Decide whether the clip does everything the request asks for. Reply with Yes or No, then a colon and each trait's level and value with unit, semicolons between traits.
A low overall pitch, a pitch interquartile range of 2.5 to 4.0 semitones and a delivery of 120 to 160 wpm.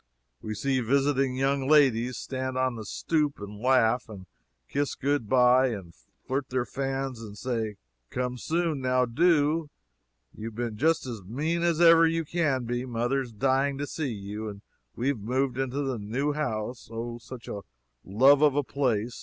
No: low, 130 Hz; average, 3.5 semitones; average, 170 wpm